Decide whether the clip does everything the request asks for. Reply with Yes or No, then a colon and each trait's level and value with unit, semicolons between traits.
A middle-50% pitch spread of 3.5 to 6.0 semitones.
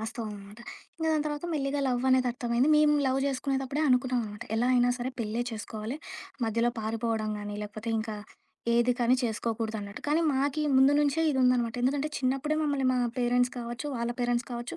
No: average, 3.1 semitones